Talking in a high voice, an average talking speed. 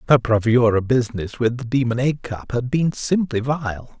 No: low, 120 Hz; average, 180 wpm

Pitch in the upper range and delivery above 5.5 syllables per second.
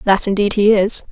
No: high, 200 Hz; 5.3 syllables/s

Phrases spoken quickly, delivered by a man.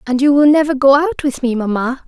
No: fast, 260 wpm; female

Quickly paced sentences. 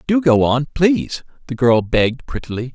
No: average, 155 wpm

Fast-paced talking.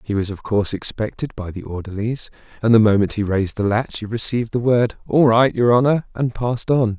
Yes: fast, 225 wpm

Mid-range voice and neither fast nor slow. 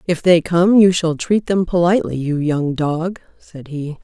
Yes: medium, 170 Hz; average, 195 wpm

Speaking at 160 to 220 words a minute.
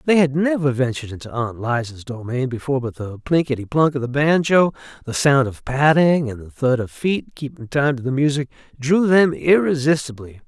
Yes: average, 190 wpm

